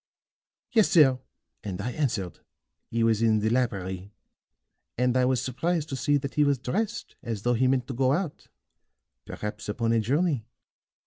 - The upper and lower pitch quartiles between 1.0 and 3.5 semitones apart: No, average, 4.1 semitones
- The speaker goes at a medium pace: Yes, average, 170 wpm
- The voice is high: No, low, 125 Hz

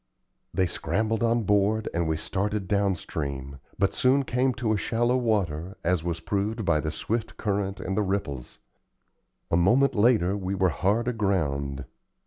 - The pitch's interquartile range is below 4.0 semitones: No, average, 4.5 semitones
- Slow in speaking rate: No, average, 155 wpm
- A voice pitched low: Yes, low, 100 Hz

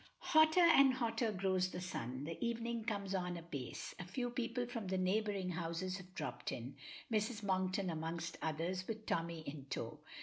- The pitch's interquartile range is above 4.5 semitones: Yes, average, 5.2 semitones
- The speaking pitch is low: No, medium, 185 Hz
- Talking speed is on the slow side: No, average, 170 wpm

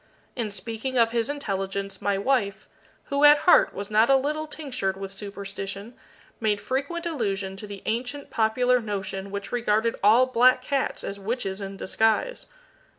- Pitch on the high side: Yes, high, 220 Hz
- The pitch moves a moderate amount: Yes, average, 4.5 semitones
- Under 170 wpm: Yes, average, 155 wpm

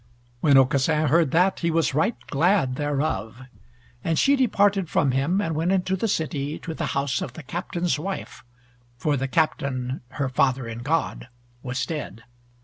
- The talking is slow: No, average, 165 wpm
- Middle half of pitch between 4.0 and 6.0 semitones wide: Yes, average, 4.3 semitones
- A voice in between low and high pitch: Yes, medium, 150 Hz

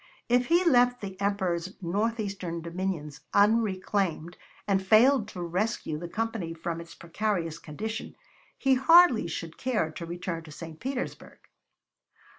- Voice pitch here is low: No, high, 195 Hz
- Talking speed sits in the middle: No, slow, 130 wpm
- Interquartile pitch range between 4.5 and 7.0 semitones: Yes, average, 5.2 semitones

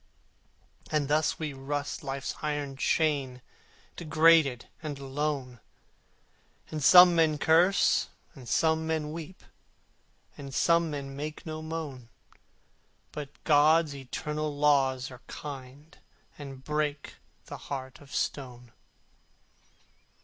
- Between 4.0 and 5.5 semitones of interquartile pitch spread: No, narrow, 2.4 semitones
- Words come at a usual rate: No, slow, 105 wpm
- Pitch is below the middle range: No, medium, 145 Hz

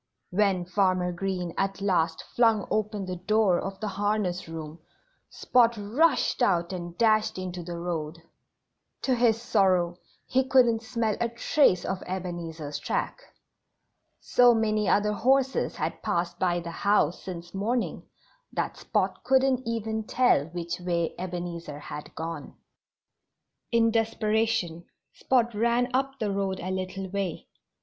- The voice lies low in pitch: No, high, 195 Hz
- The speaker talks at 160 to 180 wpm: No, slow, 135 wpm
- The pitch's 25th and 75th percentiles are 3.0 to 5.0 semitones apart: Yes, average, 4.5 semitones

